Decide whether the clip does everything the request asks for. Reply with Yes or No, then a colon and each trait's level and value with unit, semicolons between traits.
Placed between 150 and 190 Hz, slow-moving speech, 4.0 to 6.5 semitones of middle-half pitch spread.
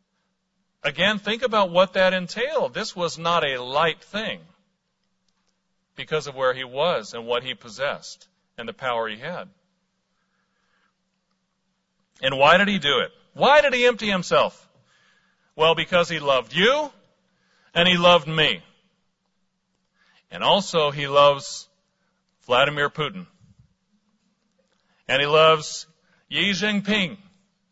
No: medium, 185 Hz; slow, 125 wpm; average, 2.9 semitones